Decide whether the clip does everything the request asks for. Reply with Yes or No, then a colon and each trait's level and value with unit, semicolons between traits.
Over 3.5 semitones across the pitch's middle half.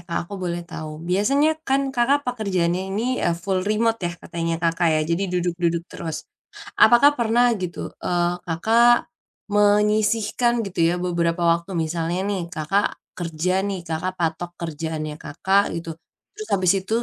Yes: average, 4.0 semitones